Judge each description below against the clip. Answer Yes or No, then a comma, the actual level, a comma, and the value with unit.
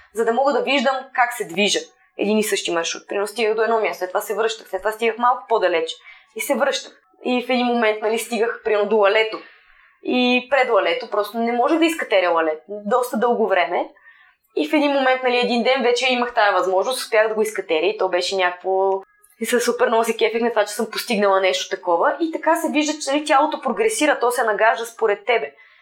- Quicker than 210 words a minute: Yes, fast, 220 wpm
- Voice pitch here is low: No, high, 230 Hz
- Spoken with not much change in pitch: No, average, 3.6 semitones